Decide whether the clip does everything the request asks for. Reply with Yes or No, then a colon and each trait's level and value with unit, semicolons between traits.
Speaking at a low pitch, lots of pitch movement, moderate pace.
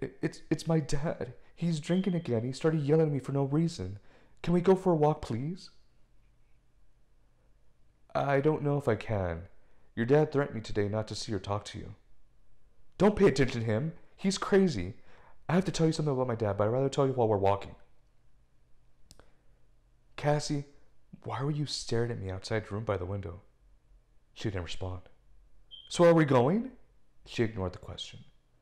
Yes: low, 130 Hz; wide, 6.9 semitones; average, 185 wpm